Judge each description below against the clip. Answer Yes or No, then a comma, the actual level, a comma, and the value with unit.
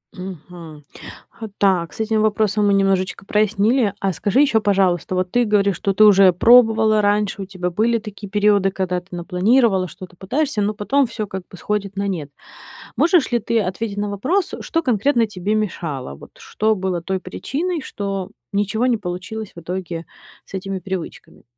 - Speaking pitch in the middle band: No, high, 200 Hz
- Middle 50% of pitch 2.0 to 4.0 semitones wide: Yes, average, 2.9 semitones